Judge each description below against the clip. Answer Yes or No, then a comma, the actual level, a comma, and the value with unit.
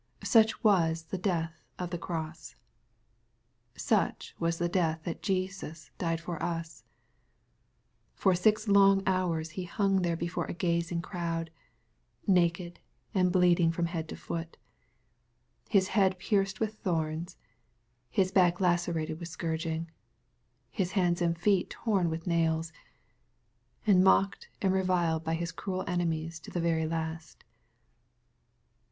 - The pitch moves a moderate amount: No, narrow, 2.2 semitones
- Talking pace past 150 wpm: No, average, 140 wpm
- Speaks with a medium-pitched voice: Yes, medium, 170 Hz